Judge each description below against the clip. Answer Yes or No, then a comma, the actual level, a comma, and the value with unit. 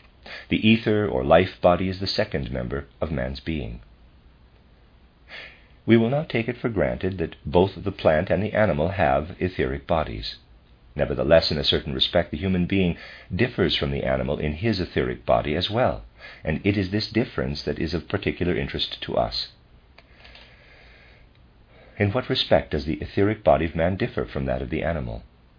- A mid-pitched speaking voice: No, very low, 80 Hz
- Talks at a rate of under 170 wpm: No, average, 175 wpm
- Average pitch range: No, wide, 6.9 semitones